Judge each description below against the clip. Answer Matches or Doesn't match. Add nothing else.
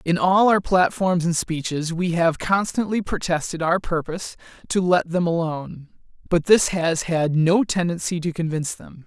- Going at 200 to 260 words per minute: Doesn't match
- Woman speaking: Doesn't match